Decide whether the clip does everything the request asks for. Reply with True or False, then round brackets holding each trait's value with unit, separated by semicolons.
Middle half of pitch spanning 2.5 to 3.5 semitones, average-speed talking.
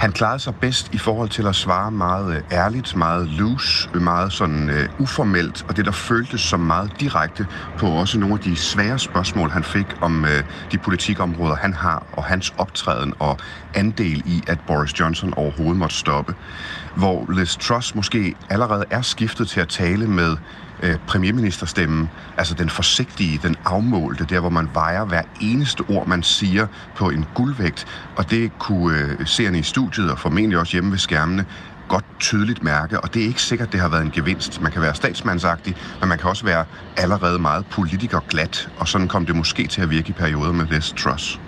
False (4.1 semitones; 190 wpm)